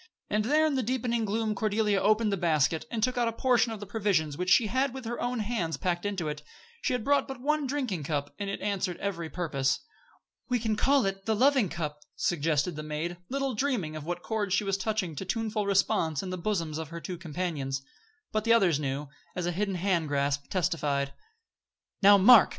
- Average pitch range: No, wide, 5.7 semitones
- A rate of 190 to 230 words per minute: Yes, fast, 205 wpm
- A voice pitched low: No, high, 195 Hz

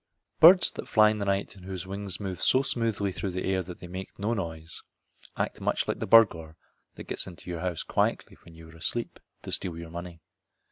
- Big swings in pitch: No, average, 3.4 semitones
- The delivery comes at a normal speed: No, fast, 220 wpm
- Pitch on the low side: Yes, very low, 95 Hz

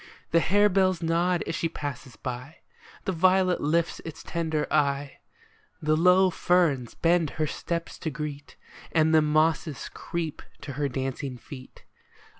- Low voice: No, medium, 160 Hz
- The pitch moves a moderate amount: Yes, average, 3.1 semitones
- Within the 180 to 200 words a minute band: No, average, 140 wpm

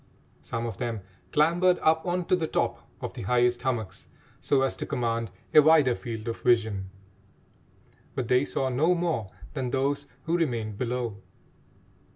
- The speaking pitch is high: No, low, 125 Hz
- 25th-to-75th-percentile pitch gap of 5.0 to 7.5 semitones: Yes, average, 5.3 semitones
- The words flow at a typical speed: Yes, average, 160 wpm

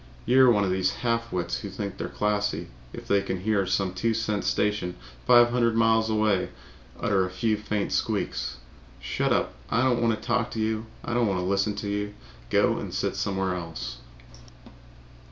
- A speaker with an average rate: Yes, average, 190 wpm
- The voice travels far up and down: No, average, 3.0 semitones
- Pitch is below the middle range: Yes, low, 105 Hz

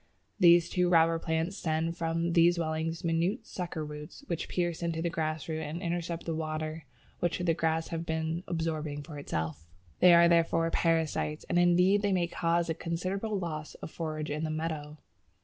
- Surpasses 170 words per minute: Yes, average, 180 wpm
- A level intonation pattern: Yes, narrow, 1.6 semitones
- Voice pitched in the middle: Yes, medium, 165 Hz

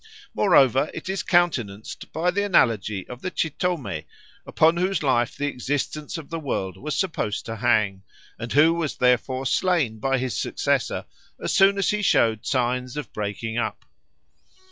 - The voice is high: No, low, 135 Hz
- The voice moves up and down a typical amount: No, wide, 6.6 semitones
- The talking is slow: No, average, 160 wpm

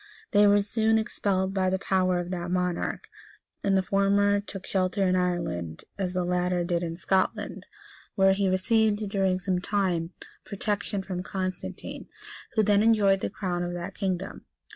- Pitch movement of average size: No, narrow, 2.0 semitones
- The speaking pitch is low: No, high, 190 Hz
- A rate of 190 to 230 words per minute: No, average, 165 wpm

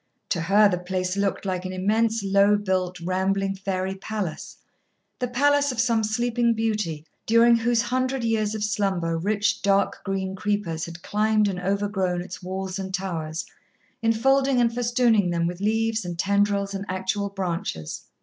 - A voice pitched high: Yes, high, 200 Hz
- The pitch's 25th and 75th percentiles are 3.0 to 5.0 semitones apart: Yes, average, 3.3 semitones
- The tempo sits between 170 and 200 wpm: No, average, 160 wpm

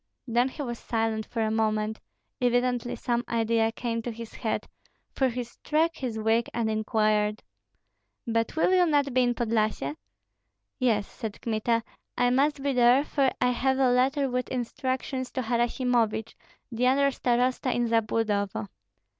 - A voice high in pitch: Yes, high, 240 Hz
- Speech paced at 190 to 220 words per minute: No, average, 155 wpm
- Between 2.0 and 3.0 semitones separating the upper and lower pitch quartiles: Yes, narrow, 2.5 semitones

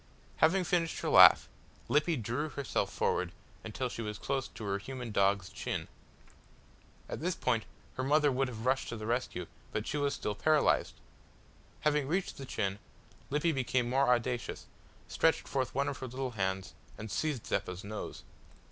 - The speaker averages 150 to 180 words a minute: Yes, average, 165 wpm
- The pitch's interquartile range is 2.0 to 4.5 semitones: No, average, 5.1 semitones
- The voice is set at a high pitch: No, low, 125 Hz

